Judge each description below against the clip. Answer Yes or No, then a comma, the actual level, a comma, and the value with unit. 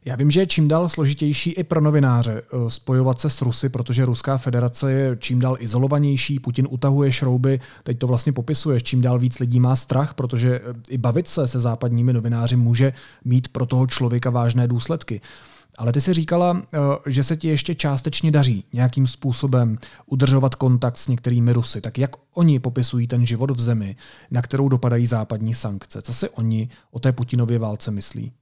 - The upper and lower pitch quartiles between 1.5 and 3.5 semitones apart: Yes, narrow, 2.5 semitones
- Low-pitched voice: Yes, low, 125 Hz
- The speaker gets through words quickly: Yes, fast, 180 wpm